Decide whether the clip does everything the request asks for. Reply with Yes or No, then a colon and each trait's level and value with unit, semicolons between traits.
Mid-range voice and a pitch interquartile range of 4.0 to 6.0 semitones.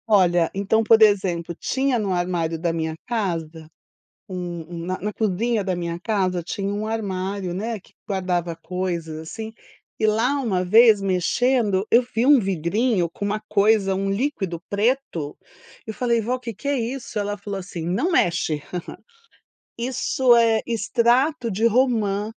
No: high, 200 Hz; average, 4.4 semitones